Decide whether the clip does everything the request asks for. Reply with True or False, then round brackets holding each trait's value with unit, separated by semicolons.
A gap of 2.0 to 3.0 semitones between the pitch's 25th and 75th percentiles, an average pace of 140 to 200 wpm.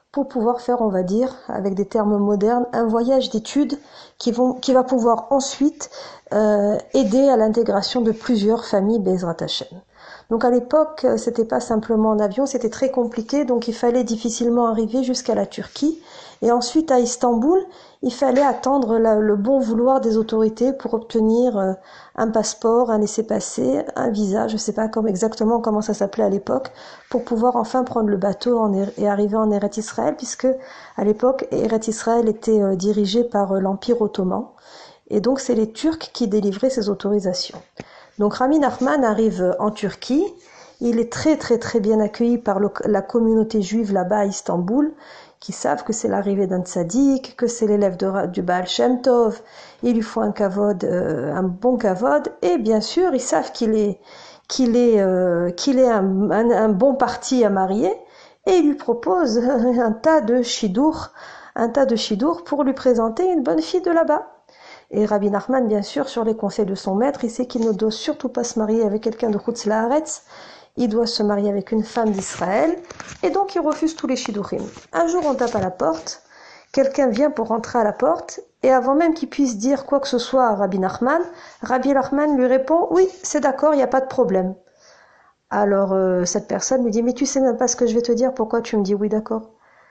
False (3.7 semitones; 195 wpm)